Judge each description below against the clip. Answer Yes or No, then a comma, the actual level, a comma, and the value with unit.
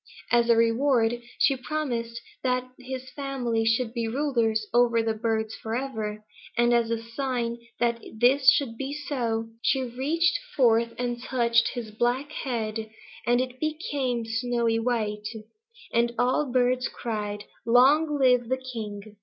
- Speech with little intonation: Yes, narrow, 2.3 semitones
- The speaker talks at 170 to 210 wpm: No, average, 145 wpm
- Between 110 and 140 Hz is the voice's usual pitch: No, high, 240 Hz